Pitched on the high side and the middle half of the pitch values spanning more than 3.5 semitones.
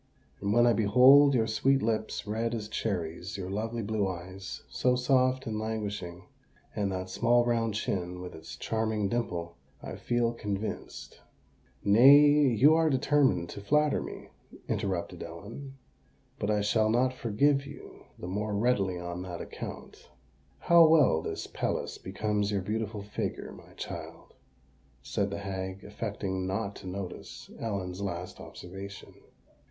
No: low, 105 Hz; average, 3.9 semitones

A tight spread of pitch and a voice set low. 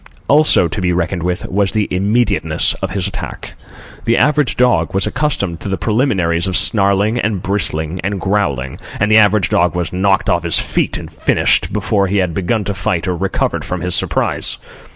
No: average, 3.0 semitones; very low, 95 Hz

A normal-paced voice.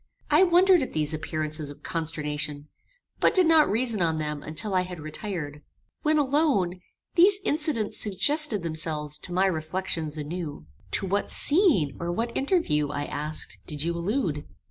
Yes: average, 155 wpm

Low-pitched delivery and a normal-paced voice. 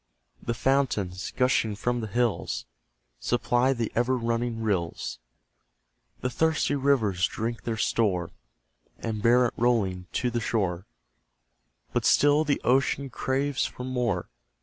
No: low, 120 Hz; slow, 125 wpm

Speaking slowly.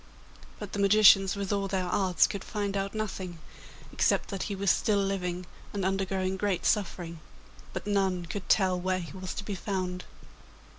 No: average, 170 wpm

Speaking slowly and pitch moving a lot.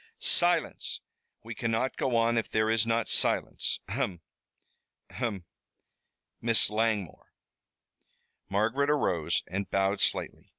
No: slow, 110 wpm; average, 2.7 semitones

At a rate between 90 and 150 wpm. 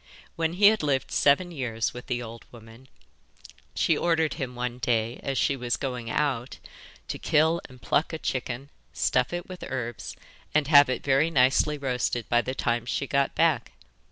No: average, 180 wpm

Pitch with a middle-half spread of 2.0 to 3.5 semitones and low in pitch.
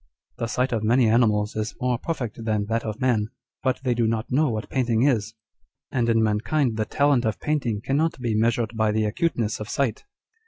Yes: average, 2.8 semitones; low, 115 Hz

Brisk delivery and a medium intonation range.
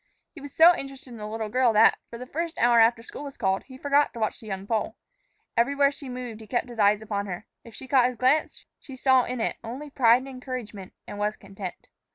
Yes: fast, 240 wpm; average, 3.6 semitones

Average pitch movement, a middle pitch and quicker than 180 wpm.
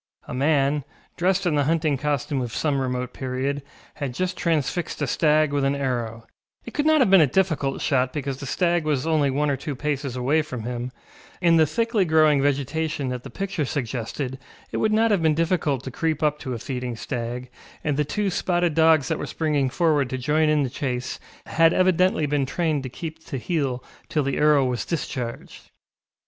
Yes: average, 3.7 semitones; medium, 145 Hz; average, 200 wpm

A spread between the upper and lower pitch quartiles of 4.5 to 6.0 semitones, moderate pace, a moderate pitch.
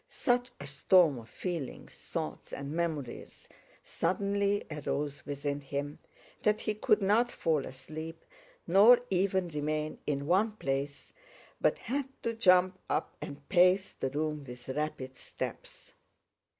No: wide, 5.6 semitones; slow, 130 wpm; medium, 155 Hz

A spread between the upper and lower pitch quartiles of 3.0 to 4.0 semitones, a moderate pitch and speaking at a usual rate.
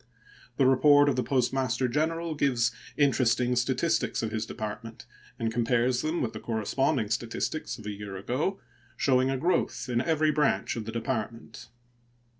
No: average, 3.7 semitones; low, 125 Hz; average, 155 wpm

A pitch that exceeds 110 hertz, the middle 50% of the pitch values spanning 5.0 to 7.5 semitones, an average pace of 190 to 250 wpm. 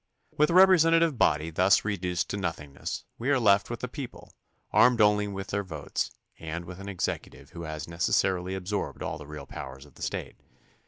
No: very low, 95 Hz; wide, 5.6 semitones; average, 195 wpm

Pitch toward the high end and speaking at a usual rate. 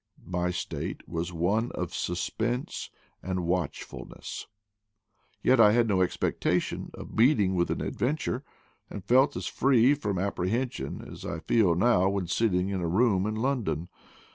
No: low, 100 Hz; average, 155 wpm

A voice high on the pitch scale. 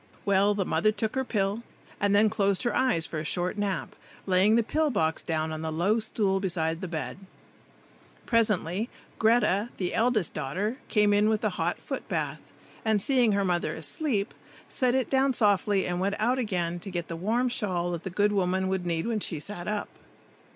Yes: high, 200 Hz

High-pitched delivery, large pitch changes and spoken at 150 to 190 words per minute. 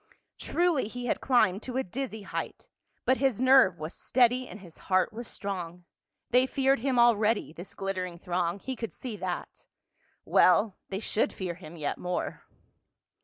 Yes: high, 215 Hz; wide, 5.7 semitones; average, 165 wpm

